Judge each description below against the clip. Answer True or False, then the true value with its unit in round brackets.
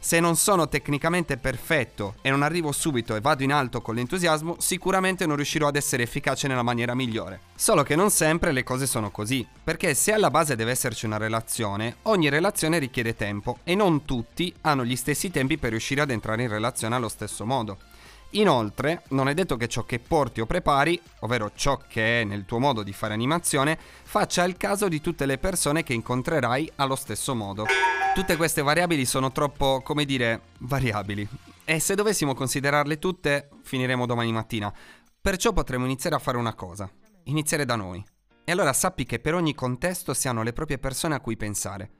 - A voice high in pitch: False (135 Hz)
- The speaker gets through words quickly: True (190 wpm)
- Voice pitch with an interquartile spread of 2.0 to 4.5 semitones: False (5.5 semitones)